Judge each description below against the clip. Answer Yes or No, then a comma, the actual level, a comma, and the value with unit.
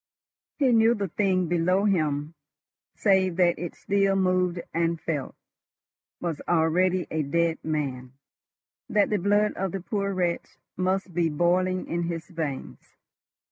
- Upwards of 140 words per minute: No, slow, 135 wpm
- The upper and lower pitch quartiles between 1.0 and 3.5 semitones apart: Yes, average, 2.9 semitones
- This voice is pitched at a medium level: Yes, medium, 175 Hz